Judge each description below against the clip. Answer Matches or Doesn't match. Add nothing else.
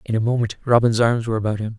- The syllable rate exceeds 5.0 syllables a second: Matches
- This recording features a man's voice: Matches